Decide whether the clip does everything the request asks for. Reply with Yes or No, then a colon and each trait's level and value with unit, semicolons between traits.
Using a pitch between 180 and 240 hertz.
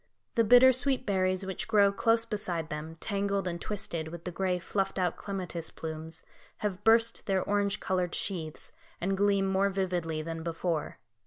Yes: high, 190 Hz